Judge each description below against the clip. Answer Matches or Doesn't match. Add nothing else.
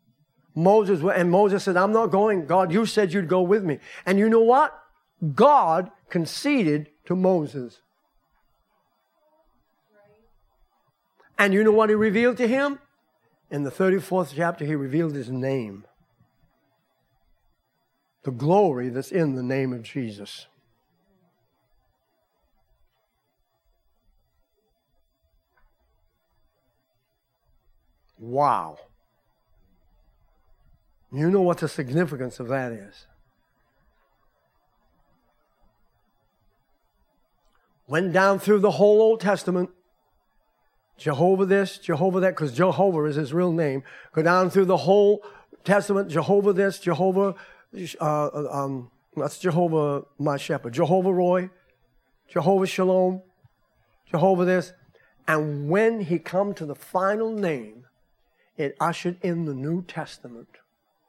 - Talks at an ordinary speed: Doesn't match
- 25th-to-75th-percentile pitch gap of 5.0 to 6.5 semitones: Matches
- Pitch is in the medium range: Matches